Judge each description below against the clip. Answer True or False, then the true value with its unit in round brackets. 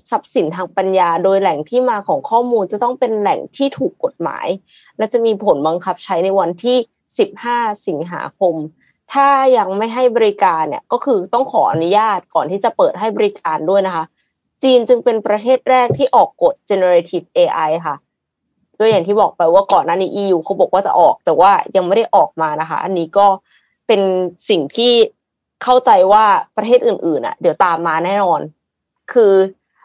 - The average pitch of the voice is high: True (210 Hz)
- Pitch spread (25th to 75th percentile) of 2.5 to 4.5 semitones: False (4.9 semitones)